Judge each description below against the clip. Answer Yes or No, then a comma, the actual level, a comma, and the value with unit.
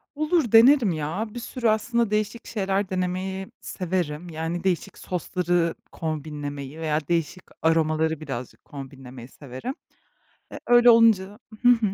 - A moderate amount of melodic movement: No, wide, 5.7 semitones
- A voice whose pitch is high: No, medium, 180 Hz